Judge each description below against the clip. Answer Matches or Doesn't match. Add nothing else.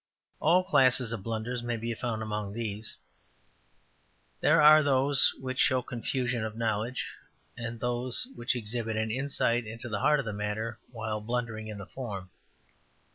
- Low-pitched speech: Matches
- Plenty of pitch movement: Doesn't match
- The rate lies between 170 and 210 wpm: Doesn't match